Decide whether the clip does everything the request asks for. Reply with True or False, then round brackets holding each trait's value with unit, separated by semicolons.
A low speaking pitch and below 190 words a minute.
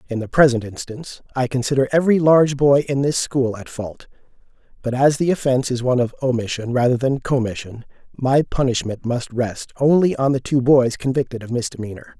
True (130 Hz; 180 wpm)